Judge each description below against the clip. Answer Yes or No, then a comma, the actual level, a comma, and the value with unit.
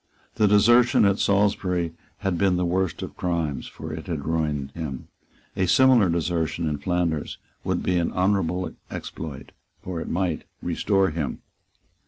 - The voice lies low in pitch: Yes, very low, 90 Hz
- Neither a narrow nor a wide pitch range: Yes, average, 3.2 semitones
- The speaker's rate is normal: Yes, average, 150 wpm